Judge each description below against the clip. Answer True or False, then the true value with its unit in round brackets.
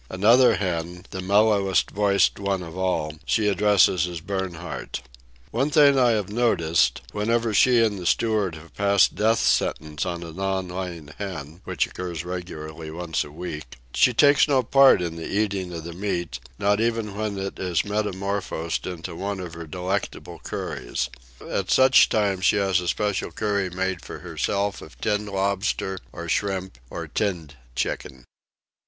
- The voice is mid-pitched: False (95 Hz)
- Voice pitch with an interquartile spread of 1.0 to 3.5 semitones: True (3.2 semitones)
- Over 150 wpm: True (160 wpm)